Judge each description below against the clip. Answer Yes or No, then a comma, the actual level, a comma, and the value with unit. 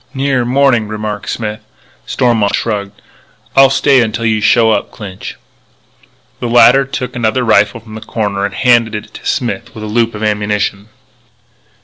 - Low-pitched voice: Yes, low, 110 Hz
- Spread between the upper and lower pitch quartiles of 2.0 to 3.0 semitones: Yes, narrow, 2.4 semitones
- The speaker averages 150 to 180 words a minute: Yes, average, 155 wpm